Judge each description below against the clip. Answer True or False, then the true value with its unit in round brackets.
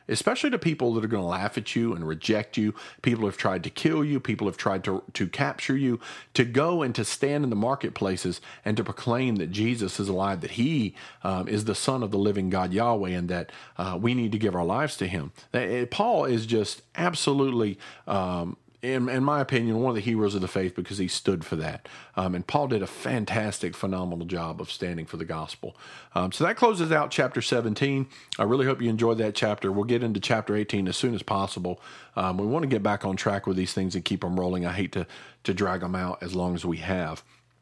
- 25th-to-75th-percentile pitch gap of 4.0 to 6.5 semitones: True (4.5 semitones)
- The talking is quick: True (235 wpm)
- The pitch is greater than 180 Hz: False (105 Hz)